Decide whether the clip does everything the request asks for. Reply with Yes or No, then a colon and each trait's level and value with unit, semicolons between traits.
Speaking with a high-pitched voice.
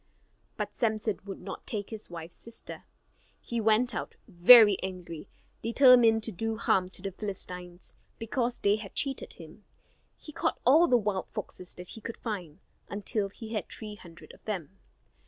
Yes: high, 210 Hz